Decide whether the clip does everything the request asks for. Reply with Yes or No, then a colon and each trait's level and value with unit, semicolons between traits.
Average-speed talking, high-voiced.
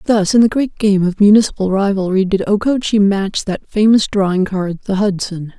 Yes: average, 185 wpm; high, 200 Hz